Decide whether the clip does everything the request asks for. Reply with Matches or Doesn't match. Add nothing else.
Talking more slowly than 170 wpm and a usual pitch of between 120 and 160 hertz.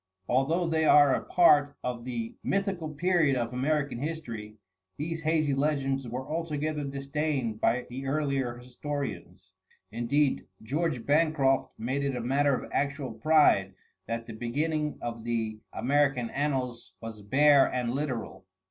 Matches